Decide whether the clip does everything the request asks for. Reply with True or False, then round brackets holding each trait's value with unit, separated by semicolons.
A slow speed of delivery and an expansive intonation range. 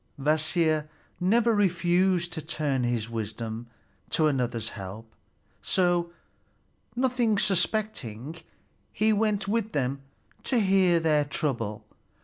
True (105 wpm; 8.1 semitones)